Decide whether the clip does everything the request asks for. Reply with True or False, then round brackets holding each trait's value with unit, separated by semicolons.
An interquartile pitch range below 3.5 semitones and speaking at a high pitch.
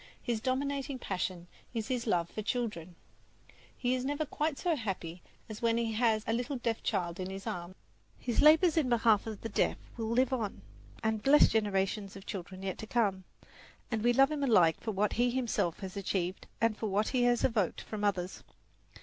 False (4.2 semitones; 220 Hz)